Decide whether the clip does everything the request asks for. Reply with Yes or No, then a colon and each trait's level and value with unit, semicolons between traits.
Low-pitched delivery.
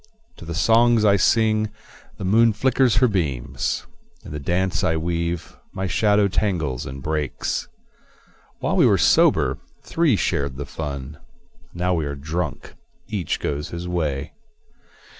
Yes: very low, 85 Hz